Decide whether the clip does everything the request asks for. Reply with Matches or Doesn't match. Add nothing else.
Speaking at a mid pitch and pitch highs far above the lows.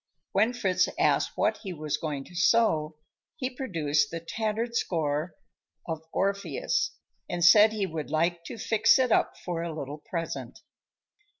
Matches